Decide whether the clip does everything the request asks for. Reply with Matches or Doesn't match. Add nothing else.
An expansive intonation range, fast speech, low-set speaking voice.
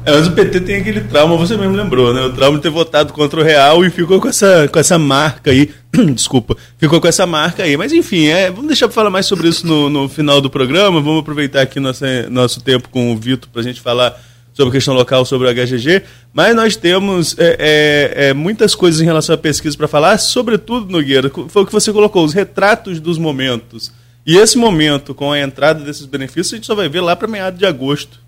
Doesn't match